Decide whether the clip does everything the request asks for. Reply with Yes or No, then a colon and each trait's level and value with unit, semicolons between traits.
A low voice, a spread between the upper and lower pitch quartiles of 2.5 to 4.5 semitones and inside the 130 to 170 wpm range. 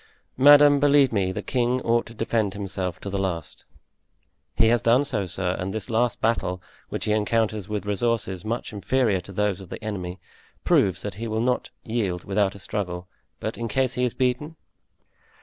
No: low, 110 Hz; average, 3.7 semitones; average, 185 wpm